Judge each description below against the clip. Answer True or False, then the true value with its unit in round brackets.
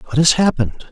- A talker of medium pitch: True (145 Hz)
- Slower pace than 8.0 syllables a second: True (5.8 syllables/s)